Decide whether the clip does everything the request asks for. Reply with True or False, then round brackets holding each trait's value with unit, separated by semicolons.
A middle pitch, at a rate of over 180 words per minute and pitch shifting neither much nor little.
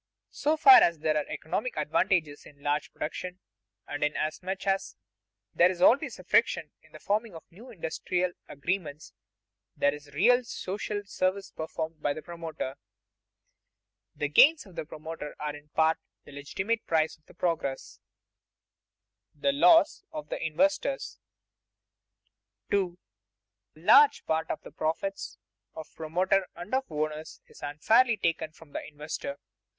False (170 Hz; 145 wpm; 5.0 semitones)